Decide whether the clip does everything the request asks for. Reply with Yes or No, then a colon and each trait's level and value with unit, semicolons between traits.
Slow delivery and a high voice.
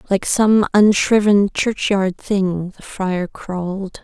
Yes: slow, 120 wpm; high, 195 Hz